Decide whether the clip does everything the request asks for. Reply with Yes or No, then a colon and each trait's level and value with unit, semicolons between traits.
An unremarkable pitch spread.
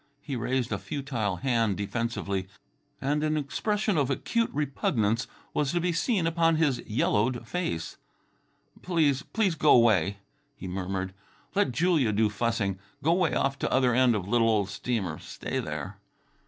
No: wide, 6.5 semitones